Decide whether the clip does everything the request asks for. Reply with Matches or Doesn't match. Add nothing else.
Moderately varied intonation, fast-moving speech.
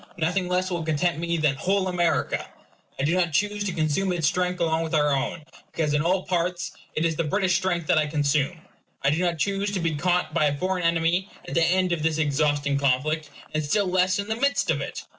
Matches